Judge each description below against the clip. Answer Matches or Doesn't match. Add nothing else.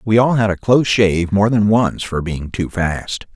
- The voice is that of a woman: Doesn't match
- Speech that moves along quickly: Matches